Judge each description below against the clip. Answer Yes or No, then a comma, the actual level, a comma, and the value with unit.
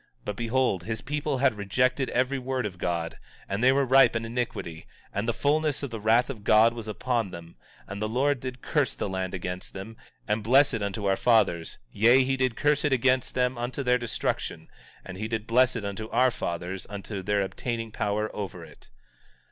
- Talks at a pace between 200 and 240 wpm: Yes, fast, 205 wpm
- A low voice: Yes, low, 115 Hz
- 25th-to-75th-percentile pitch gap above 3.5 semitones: Yes, average, 4.1 semitones